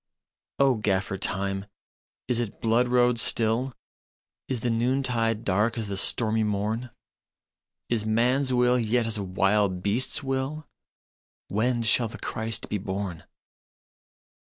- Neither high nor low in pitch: No, low, 115 Hz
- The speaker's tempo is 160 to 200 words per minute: No, average, 140 wpm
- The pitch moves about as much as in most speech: Yes, average, 3.1 semitones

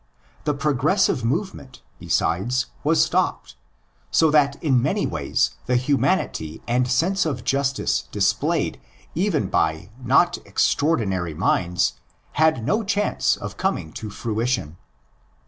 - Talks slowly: Yes, slow, 120 wpm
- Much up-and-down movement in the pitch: Yes, wide, 6.4 semitones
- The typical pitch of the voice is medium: No, low, 130 Hz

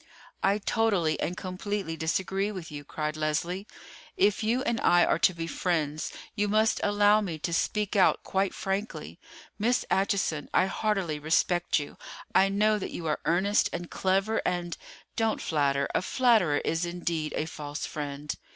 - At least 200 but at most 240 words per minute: No, average, 160 wpm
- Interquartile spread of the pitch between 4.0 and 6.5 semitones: Yes, average, 4.4 semitones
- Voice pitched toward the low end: No, medium, 185 Hz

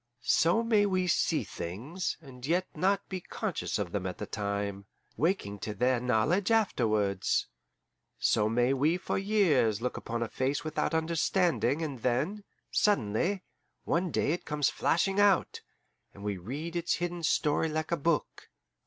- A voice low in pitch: No, medium, 150 Hz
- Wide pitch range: Yes, wide, 7.7 semitones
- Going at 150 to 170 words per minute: Yes, average, 155 wpm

